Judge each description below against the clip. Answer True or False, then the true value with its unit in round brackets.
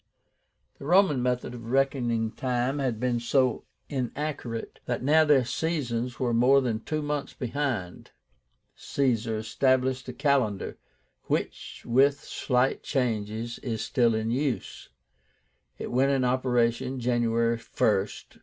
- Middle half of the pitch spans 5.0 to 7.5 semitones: False (2.7 semitones)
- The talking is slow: True (125 wpm)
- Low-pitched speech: True (125 Hz)